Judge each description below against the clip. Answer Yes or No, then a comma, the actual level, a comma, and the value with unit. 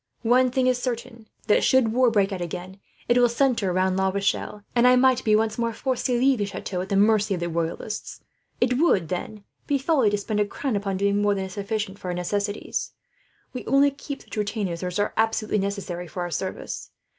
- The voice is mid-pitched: No, high, 210 Hz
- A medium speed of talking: No, fast, 220 wpm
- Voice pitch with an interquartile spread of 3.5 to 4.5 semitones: Yes, average, 4.2 semitones